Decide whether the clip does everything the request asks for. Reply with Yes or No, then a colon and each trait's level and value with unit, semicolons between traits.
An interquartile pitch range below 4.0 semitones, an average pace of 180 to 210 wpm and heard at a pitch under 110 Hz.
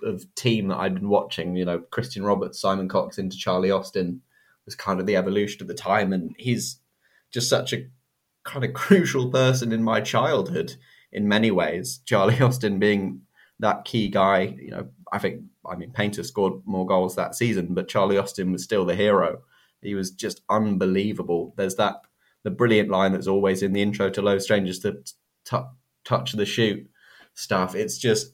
Yes: average, 2.7 semitones; average, 185 wpm; low, 100 Hz